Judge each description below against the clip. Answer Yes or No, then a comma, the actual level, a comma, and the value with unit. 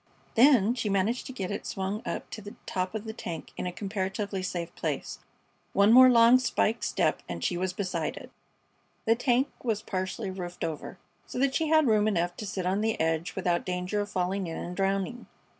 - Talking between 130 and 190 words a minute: No, fast, 205 wpm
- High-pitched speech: Yes, high, 200 Hz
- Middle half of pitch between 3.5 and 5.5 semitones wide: Yes, average, 3.8 semitones